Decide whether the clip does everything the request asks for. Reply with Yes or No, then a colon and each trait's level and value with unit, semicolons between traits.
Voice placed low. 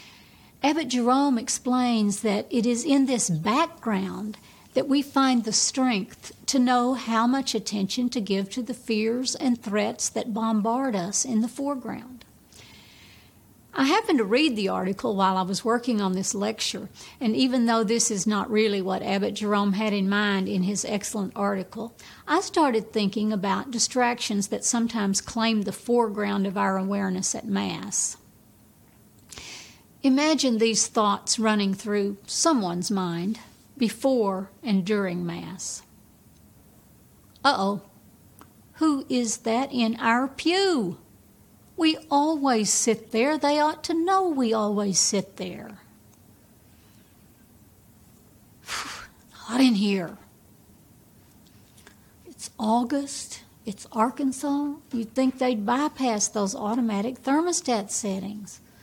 No: high, 225 Hz